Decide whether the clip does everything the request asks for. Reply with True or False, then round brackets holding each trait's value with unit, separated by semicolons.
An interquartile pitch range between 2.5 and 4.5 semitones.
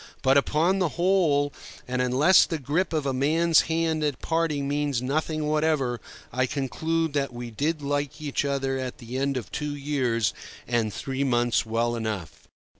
True (3.5 semitones)